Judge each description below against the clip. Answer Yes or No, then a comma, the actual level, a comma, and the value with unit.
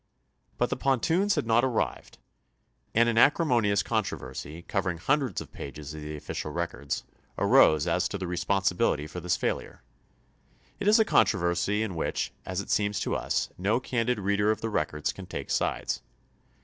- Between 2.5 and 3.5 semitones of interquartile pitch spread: No, average, 5.2 semitones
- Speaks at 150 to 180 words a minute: Yes, average, 170 wpm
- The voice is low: Yes, low, 100 Hz